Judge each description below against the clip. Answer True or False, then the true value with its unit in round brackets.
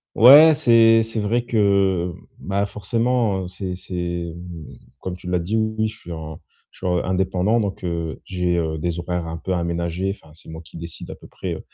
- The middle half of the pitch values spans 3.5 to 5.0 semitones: True (4.0 semitones)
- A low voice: True (90 Hz)